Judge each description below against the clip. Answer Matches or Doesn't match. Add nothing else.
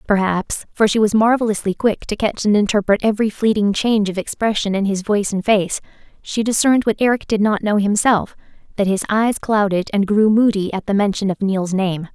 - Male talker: Doesn't match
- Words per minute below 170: Doesn't match